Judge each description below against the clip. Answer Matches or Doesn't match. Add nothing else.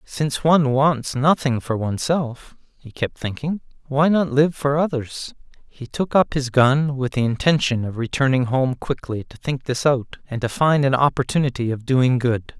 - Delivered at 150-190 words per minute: Matches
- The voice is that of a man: Matches